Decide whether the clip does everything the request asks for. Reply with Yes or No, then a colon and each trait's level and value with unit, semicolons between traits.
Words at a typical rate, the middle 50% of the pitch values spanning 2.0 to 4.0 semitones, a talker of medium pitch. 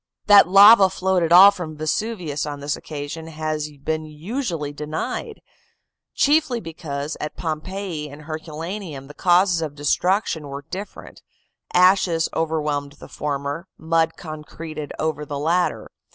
No: slow, 130 wpm; average, 3.5 semitones; medium, 160 Hz